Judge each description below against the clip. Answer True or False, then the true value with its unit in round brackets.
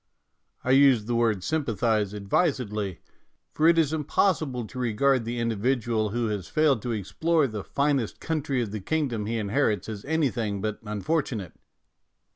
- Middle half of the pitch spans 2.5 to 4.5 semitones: False (4.9 semitones)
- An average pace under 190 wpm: True (160 wpm)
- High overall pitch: False (120 Hz)